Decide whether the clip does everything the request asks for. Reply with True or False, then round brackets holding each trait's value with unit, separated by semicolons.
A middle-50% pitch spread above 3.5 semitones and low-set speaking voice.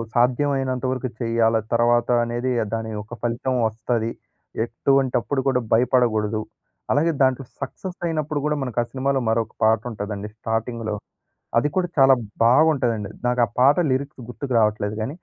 False (3.1 semitones; 120 Hz)